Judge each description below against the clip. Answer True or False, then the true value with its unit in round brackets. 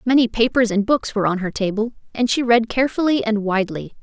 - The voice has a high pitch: True (225 Hz)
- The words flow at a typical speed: False (210 wpm)